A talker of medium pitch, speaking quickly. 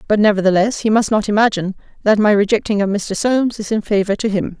No: high, 210 Hz; fast, 220 wpm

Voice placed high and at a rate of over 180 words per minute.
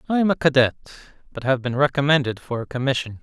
No: low, 135 Hz; fast, 205 wpm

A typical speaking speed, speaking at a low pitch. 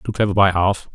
No: fast, 255 wpm; low, 100 Hz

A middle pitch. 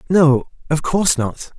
Yes: medium, 150 Hz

